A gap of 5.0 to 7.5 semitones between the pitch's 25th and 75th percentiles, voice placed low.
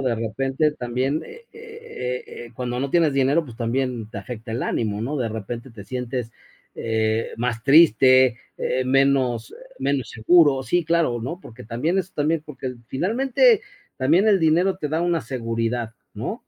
Yes: wide, 5.4 semitones; low, 130 Hz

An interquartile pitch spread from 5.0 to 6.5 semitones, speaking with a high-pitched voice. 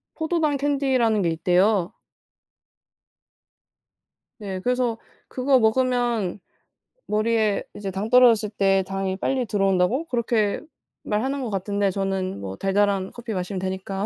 No: average, 4.2 semitones; high, 210 Hz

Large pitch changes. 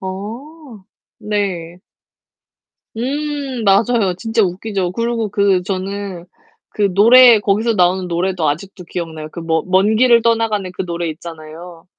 No: average, 4.2 semitones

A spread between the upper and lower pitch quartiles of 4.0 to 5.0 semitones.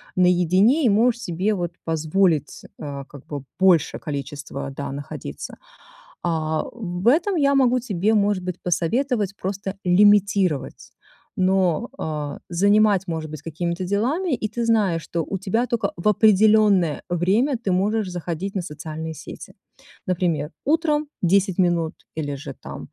Yes: average, 4.7 semitones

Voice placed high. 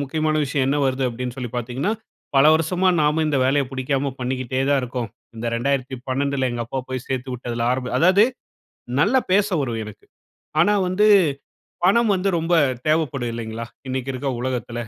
No: low, 135 Hz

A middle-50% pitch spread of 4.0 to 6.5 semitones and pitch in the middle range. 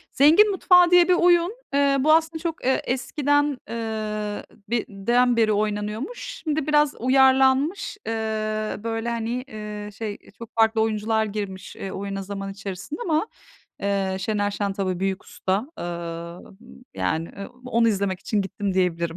No: average, 5.1 semitones; high, 220 Hz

